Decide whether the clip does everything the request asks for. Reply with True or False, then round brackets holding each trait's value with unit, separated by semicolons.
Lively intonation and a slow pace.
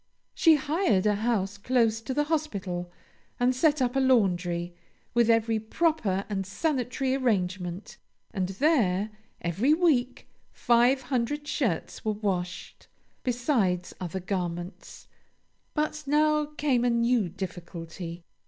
True (6.4 semitones; 120 wpm)